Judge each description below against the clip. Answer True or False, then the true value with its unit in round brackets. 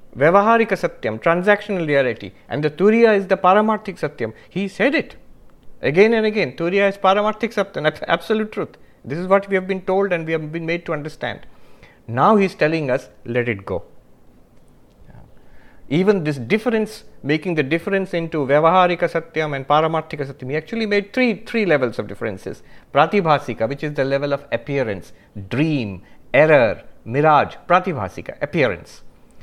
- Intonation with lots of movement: True (5.9 semitones)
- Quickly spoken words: False (160 wpm)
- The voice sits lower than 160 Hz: False (165 Hz)